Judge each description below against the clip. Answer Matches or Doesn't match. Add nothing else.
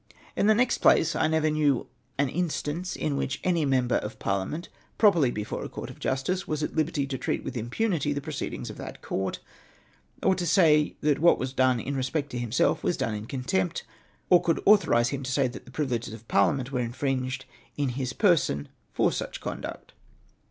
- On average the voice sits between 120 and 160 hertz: Matches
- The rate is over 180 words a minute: Matches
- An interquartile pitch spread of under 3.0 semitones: Doesn't match